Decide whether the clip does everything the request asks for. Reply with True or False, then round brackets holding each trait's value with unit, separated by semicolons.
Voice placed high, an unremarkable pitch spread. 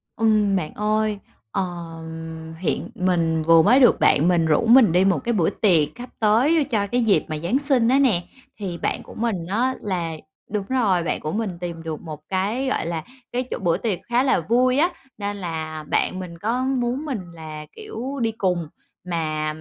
False (195 Hz; 6.0 semitones)